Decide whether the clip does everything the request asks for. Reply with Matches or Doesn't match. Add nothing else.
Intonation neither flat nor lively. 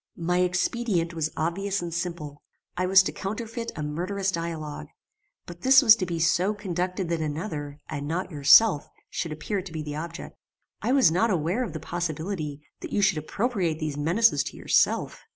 Matches